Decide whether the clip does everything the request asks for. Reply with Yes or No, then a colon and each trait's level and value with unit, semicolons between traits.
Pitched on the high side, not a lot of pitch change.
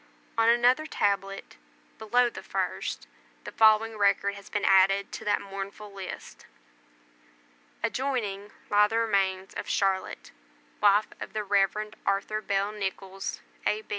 Yes: high, 205 Hz; narrow, 1.7 semitones